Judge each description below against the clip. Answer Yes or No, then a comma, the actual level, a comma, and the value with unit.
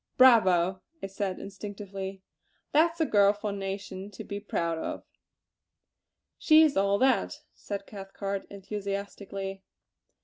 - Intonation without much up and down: Yes, narrow, 1.2 semitones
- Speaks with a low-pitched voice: No, high, 200 Hz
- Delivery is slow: Yes, slow, 125 wpm